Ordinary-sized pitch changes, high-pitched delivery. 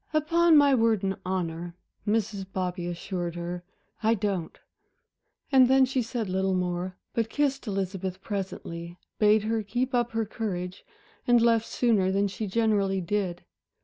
Yes: average, 3.8 semitones; high, 200 Hz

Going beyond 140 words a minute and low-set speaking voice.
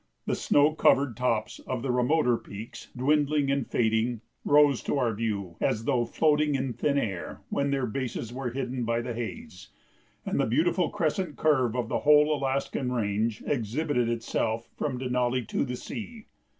Yes: average, 165 wpm; low, 125 Hz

